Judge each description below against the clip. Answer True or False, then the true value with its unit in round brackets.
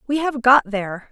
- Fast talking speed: True (215 wpm)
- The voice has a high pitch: True (245 Hz)